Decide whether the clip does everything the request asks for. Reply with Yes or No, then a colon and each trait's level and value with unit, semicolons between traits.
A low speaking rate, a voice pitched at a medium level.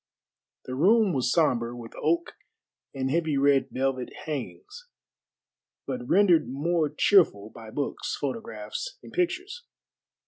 Yes: slow, 115 wpm; medium, 155 Hz